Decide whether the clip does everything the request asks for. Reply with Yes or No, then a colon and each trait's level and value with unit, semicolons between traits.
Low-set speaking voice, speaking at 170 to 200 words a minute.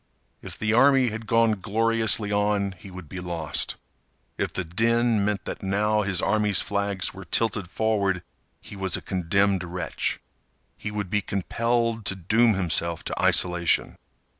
No: low, 100 Hz; average, 155 wpm